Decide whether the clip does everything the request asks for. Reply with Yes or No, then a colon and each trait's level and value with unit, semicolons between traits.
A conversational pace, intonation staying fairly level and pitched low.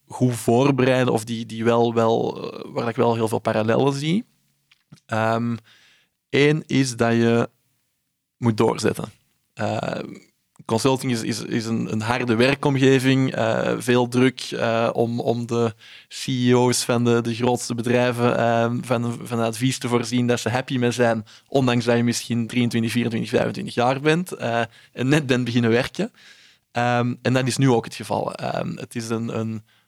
Yes: average, 165 wpm; narrow, 1.7 semitones; low, 120 Hz